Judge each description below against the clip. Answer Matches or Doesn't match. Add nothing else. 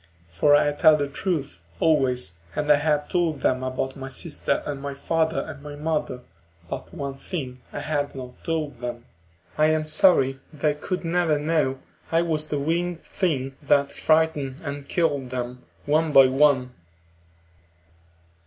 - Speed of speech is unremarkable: Matches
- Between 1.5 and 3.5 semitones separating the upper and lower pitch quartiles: Matches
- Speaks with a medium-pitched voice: Matches